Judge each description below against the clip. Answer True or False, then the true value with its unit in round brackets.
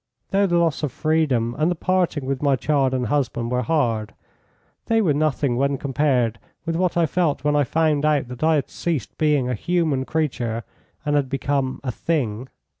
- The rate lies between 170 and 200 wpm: True (190 wpm)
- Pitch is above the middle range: False (145 Hz)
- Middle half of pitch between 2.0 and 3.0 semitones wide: False (3.9 semitones)